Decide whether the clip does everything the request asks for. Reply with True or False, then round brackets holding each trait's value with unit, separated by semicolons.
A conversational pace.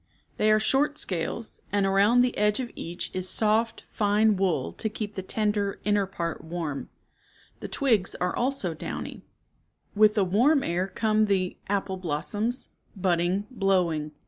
True (150 wpm)